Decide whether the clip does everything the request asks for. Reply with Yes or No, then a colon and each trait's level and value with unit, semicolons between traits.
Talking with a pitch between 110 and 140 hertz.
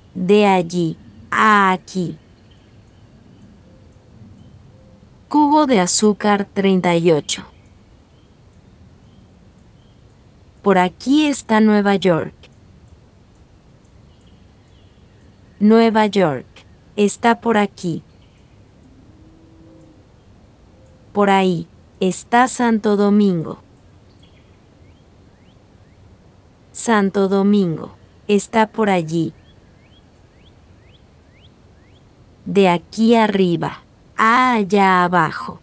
Yes: low, 135 Hz